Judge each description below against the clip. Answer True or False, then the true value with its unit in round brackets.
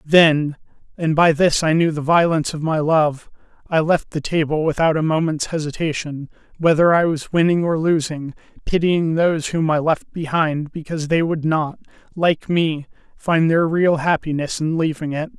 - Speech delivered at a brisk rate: False (170 wpm)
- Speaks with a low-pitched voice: False (160 Hz)